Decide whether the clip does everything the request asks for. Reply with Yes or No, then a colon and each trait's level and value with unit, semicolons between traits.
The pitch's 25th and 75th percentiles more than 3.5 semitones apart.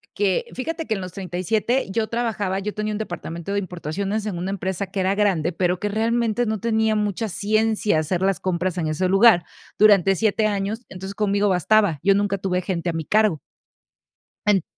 No: average, 2.9 semitones